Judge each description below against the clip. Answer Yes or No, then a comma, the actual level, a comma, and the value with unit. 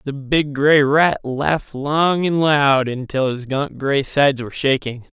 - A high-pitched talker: No, medium, 140 Hz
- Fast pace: No, average, 175 wpm